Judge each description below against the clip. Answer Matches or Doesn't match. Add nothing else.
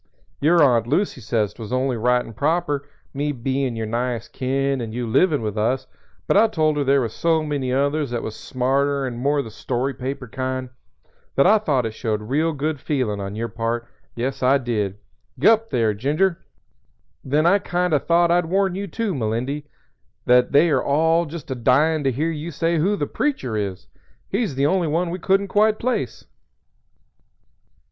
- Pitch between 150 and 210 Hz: Doesn't match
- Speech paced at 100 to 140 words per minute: Doesn't match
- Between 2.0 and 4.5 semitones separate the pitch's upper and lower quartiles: Doesn't match